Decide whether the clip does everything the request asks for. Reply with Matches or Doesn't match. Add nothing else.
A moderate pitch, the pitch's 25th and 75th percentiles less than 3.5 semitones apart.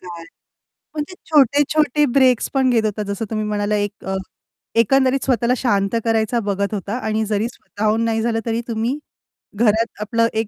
Doesn't match